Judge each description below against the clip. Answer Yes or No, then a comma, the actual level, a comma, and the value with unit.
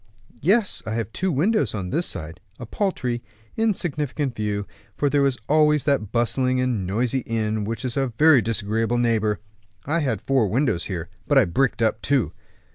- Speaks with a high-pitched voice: No, low, 125 Hz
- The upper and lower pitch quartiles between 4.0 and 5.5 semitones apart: Yes, average, 4.9 semitones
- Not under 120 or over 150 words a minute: No, average, 175 wpm